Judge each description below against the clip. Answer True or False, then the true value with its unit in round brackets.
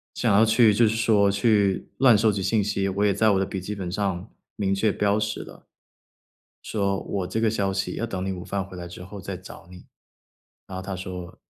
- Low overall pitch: True (100 Hz)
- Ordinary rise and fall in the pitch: False (2.1 semitones)